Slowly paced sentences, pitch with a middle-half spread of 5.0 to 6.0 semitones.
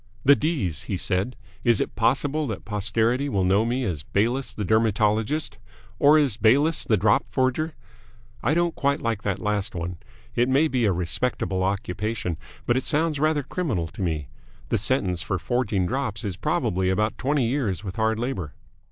No: average, 175 wpm; wide, 5.6 semitones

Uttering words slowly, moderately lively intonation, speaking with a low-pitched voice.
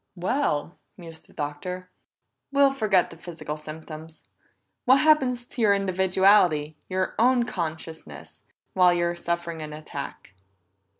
No: slow, 120 wpm; average, 4.7 semitones; medium, 180 Hz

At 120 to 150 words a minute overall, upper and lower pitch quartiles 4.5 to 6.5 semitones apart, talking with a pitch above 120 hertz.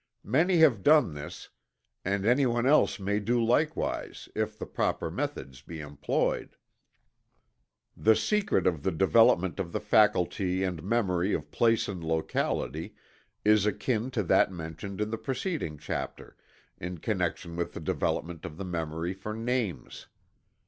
No: average, 140 wpm; wide, 5.4 semitones; low, 100 Hz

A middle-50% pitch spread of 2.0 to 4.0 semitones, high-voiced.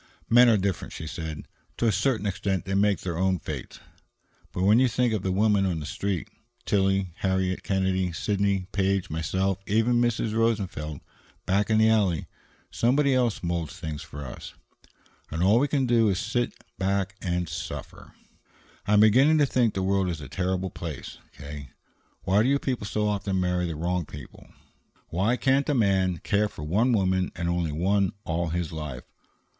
No: average, 3.7 semitones; very low, 95 Hz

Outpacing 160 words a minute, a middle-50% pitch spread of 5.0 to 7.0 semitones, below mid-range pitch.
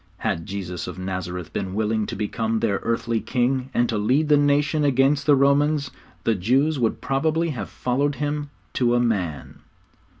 Yes: average, 170 wpm; wide, 5.4 semitones; low, 125 Hz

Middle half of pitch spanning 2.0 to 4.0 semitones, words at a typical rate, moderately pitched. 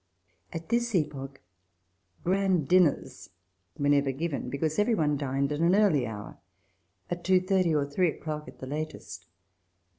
No: average, 4.6 semitones; average, 160 wpm; medium, 155 Hz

